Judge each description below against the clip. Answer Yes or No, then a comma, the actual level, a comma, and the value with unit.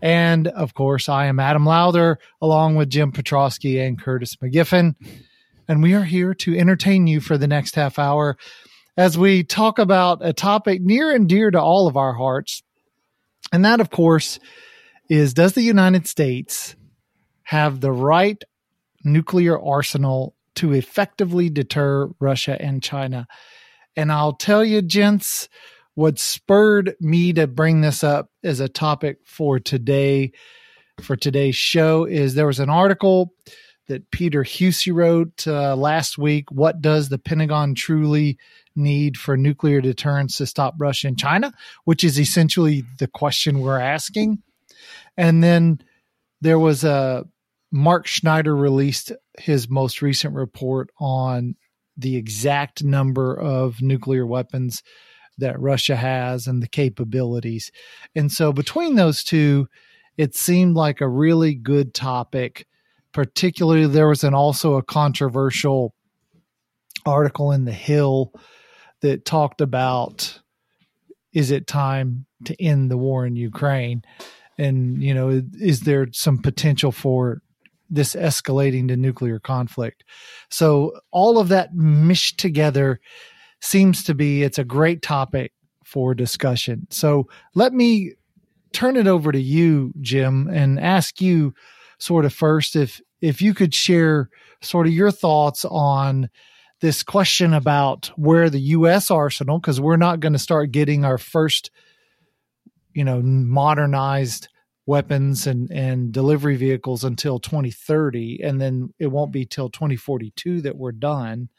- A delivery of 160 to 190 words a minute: No, average, 140 wpm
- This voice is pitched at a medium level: Yes, medium, 150 Hz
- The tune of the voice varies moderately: Yes, average, 3.8 semitones